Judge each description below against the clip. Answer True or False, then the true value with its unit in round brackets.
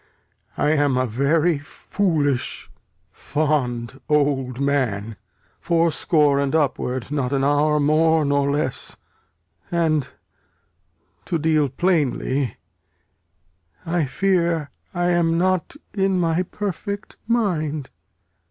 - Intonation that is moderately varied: True (3.3 semitones)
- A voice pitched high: False (150 Hz)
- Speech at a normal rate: False (95 wpm)